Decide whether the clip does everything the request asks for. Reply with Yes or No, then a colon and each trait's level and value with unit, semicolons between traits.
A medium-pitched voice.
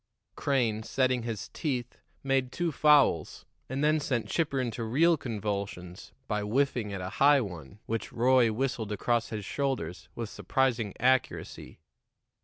No: low, 120 Hz